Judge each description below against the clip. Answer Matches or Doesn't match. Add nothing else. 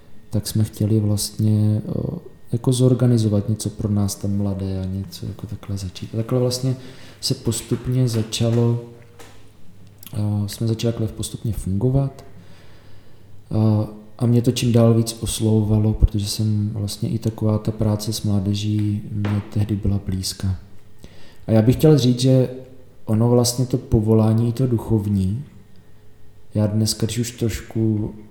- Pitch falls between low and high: Doesn't match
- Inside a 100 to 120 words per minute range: Doesn't match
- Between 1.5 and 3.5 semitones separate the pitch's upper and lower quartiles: Matches